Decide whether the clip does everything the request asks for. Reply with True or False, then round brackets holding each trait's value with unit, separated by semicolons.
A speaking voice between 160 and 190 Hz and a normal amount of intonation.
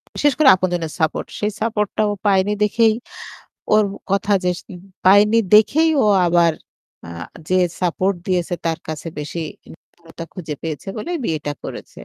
True (185 Hz; 4.1 semitones)